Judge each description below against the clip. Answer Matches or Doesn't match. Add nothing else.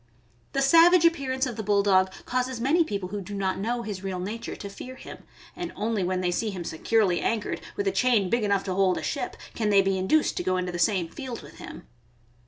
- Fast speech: Matches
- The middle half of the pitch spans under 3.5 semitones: Doesn't match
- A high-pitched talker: Matches